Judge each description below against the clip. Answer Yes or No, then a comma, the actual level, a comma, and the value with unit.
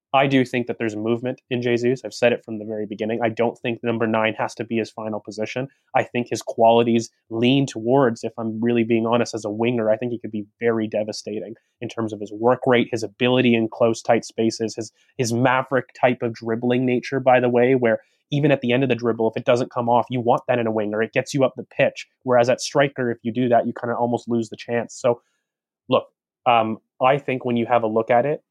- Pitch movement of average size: No, narrow, 1.8 semitones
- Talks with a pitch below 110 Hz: No, low, 120 Hz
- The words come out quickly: Yes, fast, 255 wpm